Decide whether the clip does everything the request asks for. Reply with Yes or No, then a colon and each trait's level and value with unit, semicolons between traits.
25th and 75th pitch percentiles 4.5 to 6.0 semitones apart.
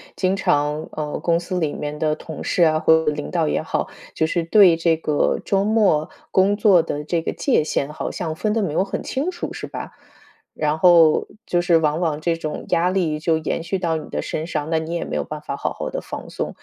No: average, 2.8 semitones